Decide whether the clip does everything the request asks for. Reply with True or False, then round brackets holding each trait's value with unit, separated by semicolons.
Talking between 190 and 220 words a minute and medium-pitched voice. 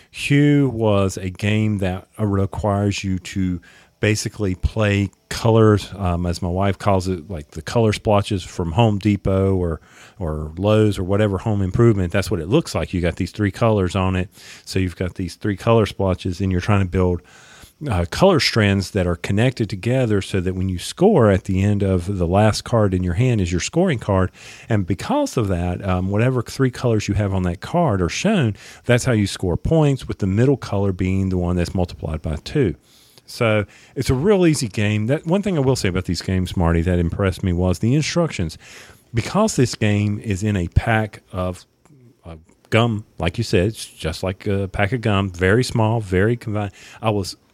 False (200 wpm; 100 Hz)